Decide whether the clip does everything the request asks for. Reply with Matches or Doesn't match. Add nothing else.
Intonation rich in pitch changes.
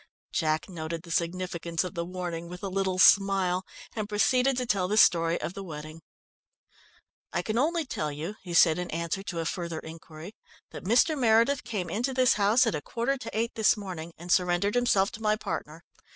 Doesn't match